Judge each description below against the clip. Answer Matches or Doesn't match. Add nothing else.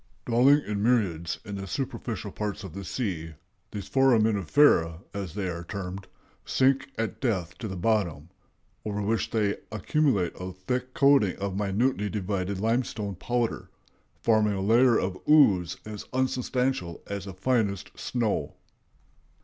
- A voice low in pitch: Matches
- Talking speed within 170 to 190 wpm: Doesn't match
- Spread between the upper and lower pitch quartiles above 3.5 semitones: Matches